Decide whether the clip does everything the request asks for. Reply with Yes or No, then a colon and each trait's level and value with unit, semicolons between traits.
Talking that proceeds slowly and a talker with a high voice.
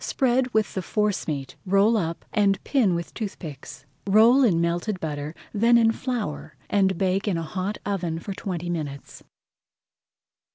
No: average, 150 wpm; high, 195 Hz